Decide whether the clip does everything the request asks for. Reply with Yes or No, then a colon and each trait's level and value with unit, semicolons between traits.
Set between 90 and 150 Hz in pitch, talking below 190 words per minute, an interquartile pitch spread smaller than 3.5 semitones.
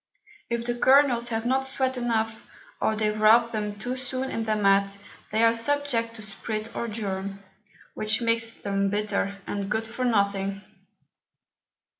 No: high, 225 Hz; average, 155 wpm; narrow, 2.6 semitones